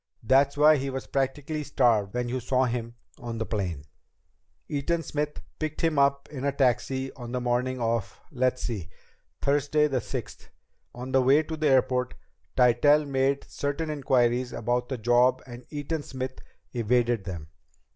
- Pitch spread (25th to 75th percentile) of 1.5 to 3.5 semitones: Yes, average, 2.7 semitones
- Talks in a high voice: No, low, 130 Hz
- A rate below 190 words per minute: Yes, average, 160 wpm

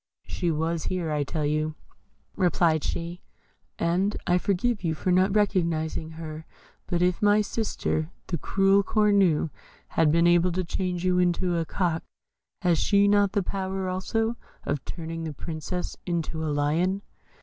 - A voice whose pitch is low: No, medium, 175 Hz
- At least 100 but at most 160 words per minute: Yes, average, 155 wpm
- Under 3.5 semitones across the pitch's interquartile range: Yes, average, 3.0 semitones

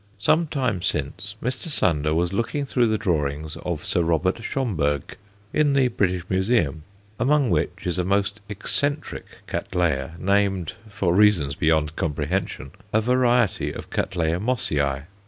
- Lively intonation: Yes, wide, 6.7 semitones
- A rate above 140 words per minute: No, slow, 135 wpm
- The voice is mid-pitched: No, very low, 95 Hz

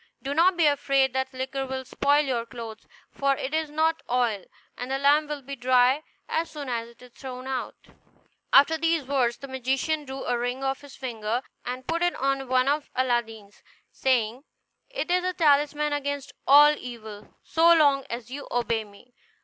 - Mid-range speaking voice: No, very high, 265 Hz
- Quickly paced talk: No, average, 190 wpm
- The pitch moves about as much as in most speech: Yes, average, 3.0 semitones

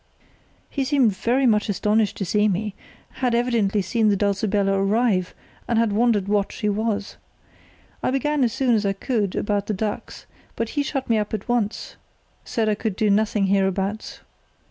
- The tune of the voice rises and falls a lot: No, average, 2.7 semitones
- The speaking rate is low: No, average, 175 wpm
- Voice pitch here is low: No, high, 215 Hz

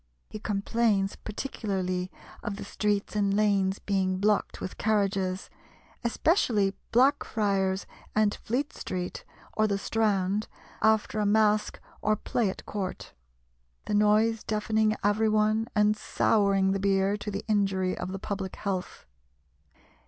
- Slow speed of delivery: Yes, slow, 130 wpm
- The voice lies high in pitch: Yes, high, 205 Hz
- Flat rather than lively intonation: Yes, narrow, 1.8 semitones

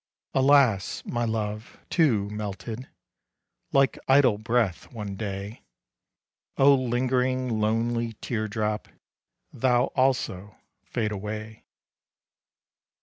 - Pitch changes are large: No, average, 3.3 semitones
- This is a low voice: Yes, low, 115 Hz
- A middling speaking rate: No, slow, 90 wpm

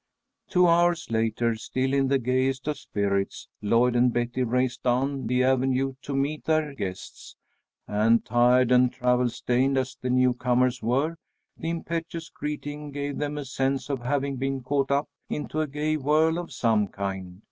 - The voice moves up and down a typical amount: Yes, average, 3.0 semitones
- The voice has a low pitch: Yes, low, 130 Hz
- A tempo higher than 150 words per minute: Yes, average, 165 wpm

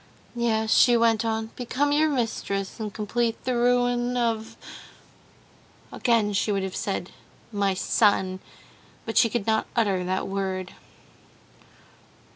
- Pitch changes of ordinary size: Yes, average, 3.2 semitones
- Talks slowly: Yes, slow, 125 wpm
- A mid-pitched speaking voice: No, high, 220 Hz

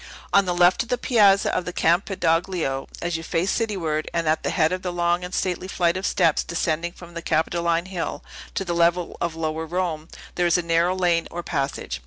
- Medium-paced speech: No, fast, 215 wpm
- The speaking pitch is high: No, medium, 170 Hz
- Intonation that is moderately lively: No, narrow, 1.8 semitones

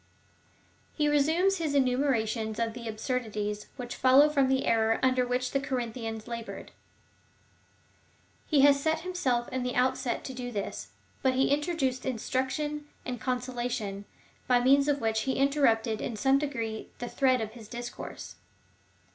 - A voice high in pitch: Yes, very high, 255 Hz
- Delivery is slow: No, average, 155 wpm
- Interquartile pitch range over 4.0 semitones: No, average, 3.2 semitones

